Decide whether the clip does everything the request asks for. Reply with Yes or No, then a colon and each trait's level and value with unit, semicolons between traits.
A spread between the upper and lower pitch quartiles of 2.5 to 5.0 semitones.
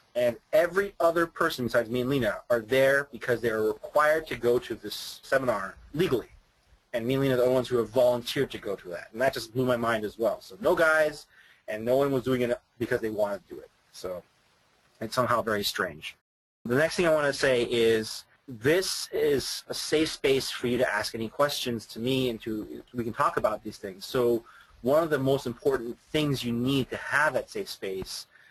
Yes: average, 3.7 semitones